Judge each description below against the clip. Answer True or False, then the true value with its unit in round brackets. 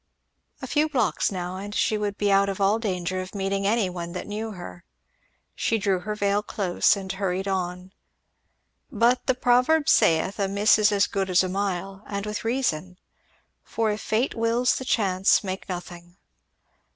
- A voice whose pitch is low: False (200 Hz)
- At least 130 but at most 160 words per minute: False (175 wpm)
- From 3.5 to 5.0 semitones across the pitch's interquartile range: False (2.7 semitones)